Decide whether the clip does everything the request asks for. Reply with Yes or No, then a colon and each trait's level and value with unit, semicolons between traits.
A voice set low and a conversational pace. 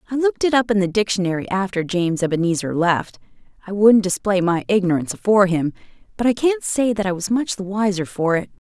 No: high, 195 Hz; average, 195 wpm